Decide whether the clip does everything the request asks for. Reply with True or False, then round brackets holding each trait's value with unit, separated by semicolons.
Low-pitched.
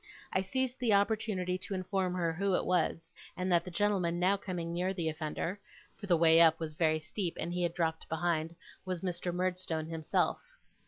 False (175 Hz)